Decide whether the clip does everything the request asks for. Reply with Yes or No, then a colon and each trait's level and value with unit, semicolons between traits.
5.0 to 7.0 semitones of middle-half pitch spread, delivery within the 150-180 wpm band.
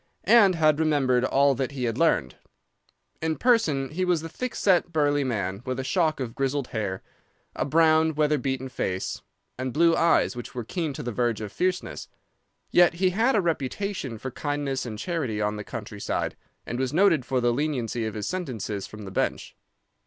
No: wide, 5.4 semitones; average, 190 wpm